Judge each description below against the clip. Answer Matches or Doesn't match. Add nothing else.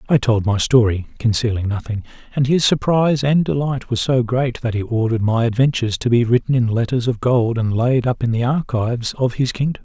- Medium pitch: Doesn't match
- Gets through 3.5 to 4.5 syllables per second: Doesn't match